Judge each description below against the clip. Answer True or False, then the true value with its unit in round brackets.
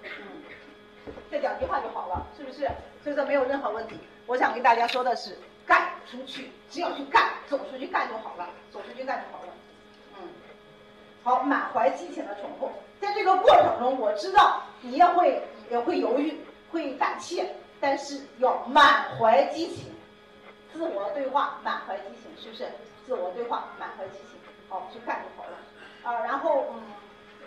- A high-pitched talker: True (280 Hz)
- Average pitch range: True (4.7 semitones)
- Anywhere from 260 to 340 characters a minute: False (245 characters per minute)